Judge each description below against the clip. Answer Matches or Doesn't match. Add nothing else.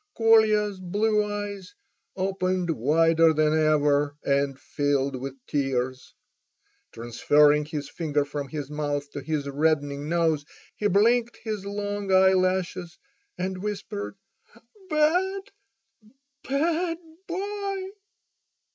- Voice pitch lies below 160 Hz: Doesn't match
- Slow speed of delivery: Matches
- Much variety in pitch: Matches